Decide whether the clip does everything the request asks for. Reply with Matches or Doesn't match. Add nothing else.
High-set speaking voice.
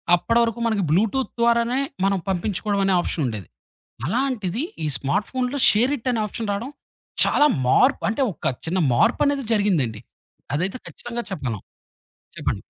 Matches